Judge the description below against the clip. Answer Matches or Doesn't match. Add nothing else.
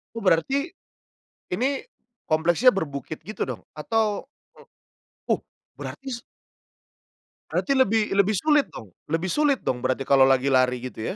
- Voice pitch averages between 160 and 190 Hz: Matches